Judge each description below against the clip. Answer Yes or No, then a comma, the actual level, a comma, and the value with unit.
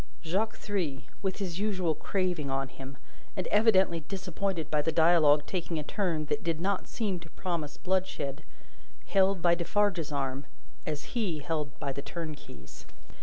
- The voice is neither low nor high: Yes, medium, 170 Hz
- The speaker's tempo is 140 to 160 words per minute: Yes, average, 155 wpm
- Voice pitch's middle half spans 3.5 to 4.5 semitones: Yes, average, 4.2 semitones